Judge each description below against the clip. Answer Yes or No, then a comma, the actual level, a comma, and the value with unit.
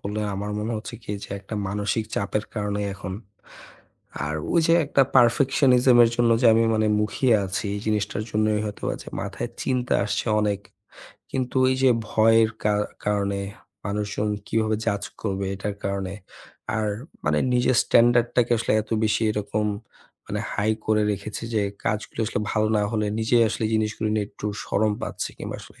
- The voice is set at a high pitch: No, low, 105 Hz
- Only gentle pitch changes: Yes, narrow, 2.0 semitones